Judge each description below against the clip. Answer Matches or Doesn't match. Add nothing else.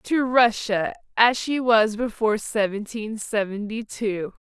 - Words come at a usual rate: Doesn't match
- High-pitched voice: Matches